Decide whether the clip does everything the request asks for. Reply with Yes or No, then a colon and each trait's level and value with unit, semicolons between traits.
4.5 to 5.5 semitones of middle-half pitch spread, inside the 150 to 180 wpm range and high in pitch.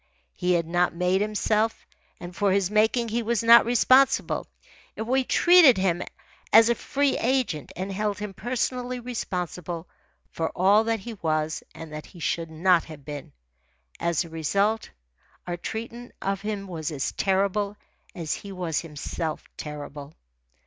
Yes: average, 5.2 semitones; average, 155 wpm; high, 195 Hz